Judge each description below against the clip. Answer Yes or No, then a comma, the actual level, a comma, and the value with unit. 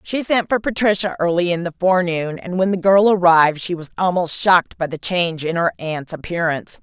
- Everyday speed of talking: No, fast, 210 wpm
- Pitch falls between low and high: Yes, medium, 175 Hz